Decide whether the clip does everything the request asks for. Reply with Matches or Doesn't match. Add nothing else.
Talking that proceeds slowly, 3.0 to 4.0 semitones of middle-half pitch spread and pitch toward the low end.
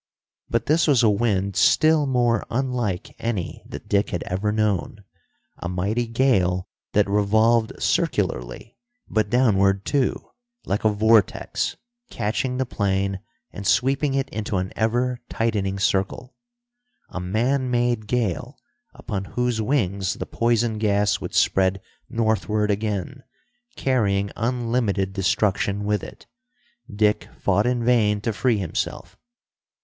Matches